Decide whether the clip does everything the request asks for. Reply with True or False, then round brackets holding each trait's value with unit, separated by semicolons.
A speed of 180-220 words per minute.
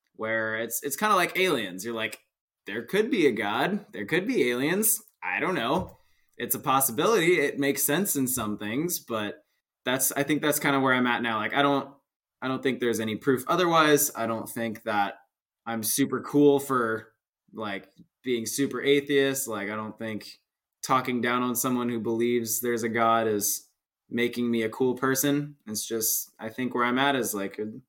True (195 wpm)